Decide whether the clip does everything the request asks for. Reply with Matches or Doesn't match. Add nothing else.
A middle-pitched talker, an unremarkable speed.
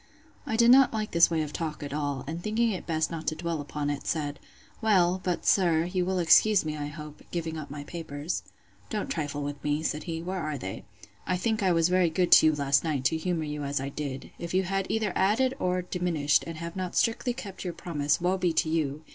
Doesn't match